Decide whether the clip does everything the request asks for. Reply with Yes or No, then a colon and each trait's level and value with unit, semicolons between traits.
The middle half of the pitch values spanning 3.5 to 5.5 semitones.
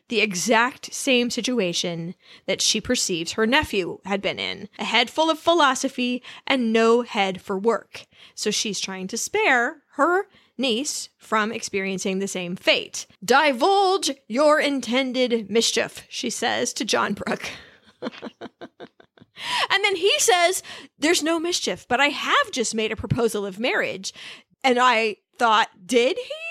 Yes: average, 5.1 semitones